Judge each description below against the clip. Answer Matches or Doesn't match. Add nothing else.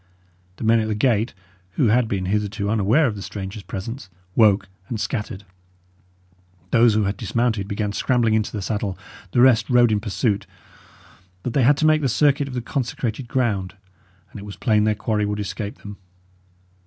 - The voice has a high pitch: Doesn't match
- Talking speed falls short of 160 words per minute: Doesn't match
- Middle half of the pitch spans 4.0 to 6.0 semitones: Doesn't match